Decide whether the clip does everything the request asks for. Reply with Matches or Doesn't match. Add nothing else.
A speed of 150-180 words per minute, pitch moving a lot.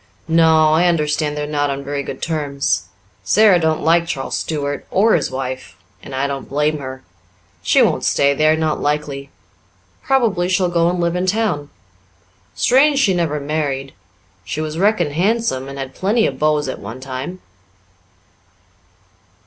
Doesn't match